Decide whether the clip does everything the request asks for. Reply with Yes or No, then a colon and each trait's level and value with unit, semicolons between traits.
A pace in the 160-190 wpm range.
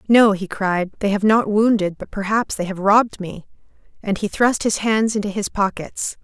No: average, 200 wpm